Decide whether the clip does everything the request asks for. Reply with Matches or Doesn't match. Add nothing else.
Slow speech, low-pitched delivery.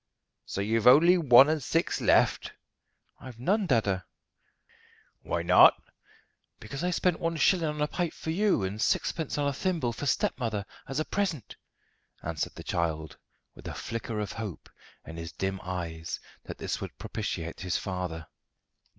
Doesn't match